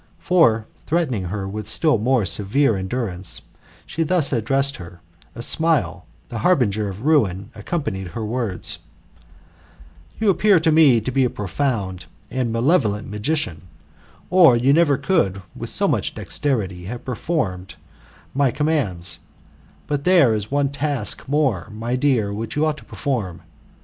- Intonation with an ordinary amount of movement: No, wide, 6.4 semitones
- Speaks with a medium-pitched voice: No, low, 120 Hz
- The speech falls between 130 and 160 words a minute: Yes, average, 145 wpm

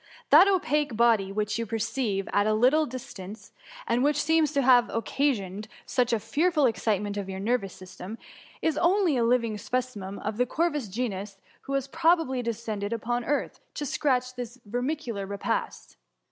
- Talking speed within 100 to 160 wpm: No, average, 170 wpm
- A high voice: Yes, high, 240 Hz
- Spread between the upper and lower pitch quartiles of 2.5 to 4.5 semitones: No, average, 5.1 semitones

